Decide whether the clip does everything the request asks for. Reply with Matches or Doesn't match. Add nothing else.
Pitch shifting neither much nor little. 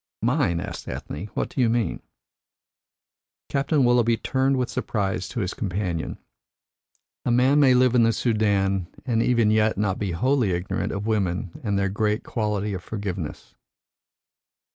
Matches